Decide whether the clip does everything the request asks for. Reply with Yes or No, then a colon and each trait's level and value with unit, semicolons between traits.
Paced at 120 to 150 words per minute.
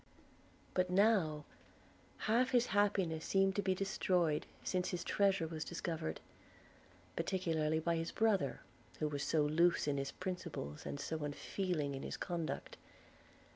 Yes: slow, 135 wpm